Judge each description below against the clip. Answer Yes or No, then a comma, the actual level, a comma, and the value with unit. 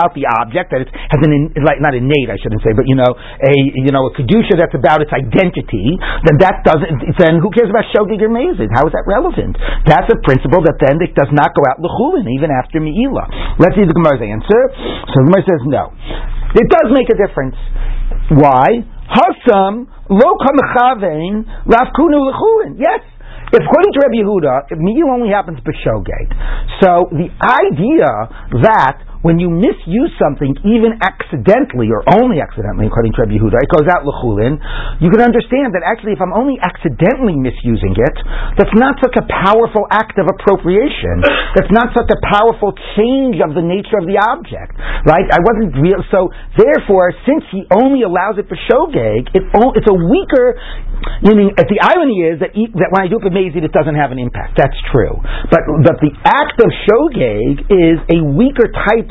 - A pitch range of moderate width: No, wide, 7.2 semitones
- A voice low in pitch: No, medium, 185 Hz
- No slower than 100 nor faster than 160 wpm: No, average, 180 wpm